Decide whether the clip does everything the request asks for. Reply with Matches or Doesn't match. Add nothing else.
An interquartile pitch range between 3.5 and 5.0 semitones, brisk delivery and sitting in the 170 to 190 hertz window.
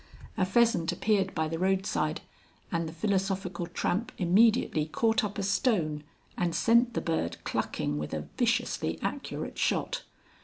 Doesn't match